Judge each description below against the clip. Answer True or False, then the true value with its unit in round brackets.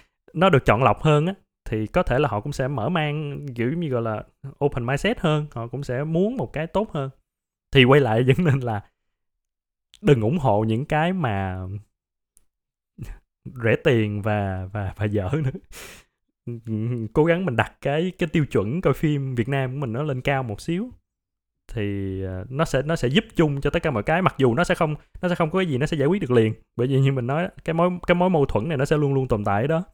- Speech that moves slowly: False (230 wpm)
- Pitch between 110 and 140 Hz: True (135 Hz)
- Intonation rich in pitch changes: True (6.8 semitones)